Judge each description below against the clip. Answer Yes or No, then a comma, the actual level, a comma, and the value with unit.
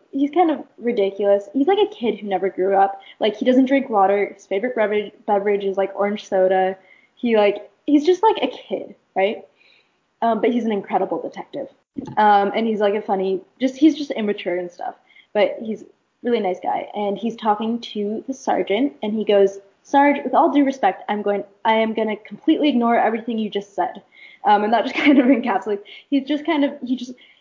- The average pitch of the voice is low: No, high, 215 Hz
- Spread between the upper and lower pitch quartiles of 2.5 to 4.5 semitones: No, average, 5.1 semitones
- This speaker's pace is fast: Yes, fast, 210 wpm